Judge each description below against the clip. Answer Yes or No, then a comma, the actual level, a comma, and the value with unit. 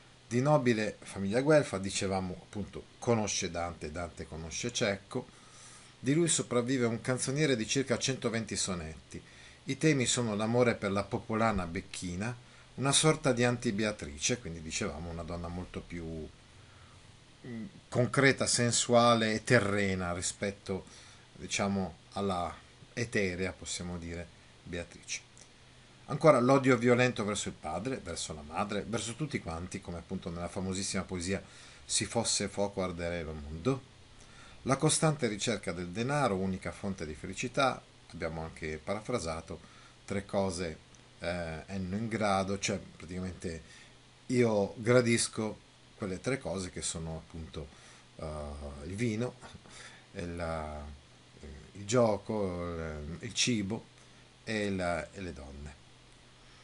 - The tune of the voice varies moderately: No, wide, 5.7 semitones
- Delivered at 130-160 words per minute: No, average, 120 wpm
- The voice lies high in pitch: No, low, 100 Hz